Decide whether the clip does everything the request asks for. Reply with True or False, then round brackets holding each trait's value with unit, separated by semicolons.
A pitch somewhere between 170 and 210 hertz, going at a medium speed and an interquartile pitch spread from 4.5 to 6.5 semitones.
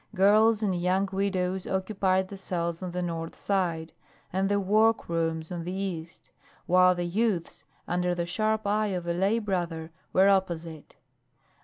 False (185 Hz; 160 wpm; 2.5 semitones)